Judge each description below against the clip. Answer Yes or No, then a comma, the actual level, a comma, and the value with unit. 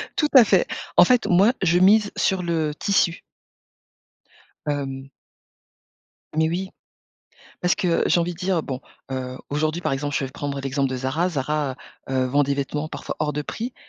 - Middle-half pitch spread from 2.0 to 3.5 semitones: No, average, 4.7 semitones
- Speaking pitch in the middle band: Yes, medium, 155 Hz